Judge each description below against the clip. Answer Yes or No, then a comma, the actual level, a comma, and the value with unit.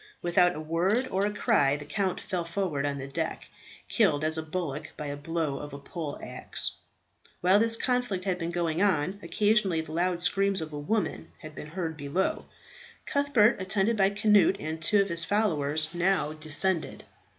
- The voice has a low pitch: No, medium, 175 Hz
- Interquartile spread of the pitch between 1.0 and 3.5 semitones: No, average, 4.3 semitones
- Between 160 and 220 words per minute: Yes, average, 185 wpm